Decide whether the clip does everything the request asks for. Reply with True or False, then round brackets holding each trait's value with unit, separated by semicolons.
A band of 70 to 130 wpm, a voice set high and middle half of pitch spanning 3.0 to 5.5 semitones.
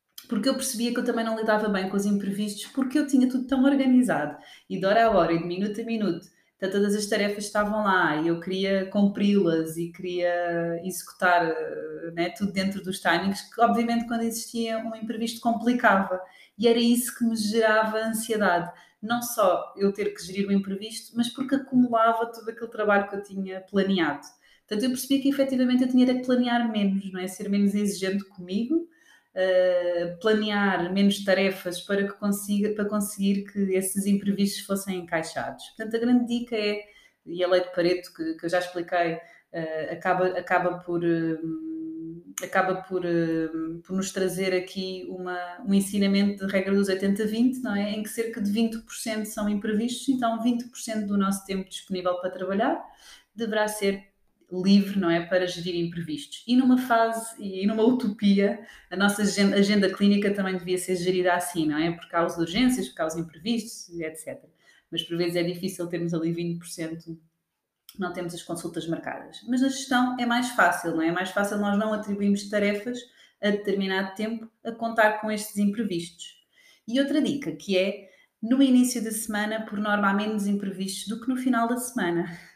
False (180 wpm; 200 Hz; 3.9 semitones)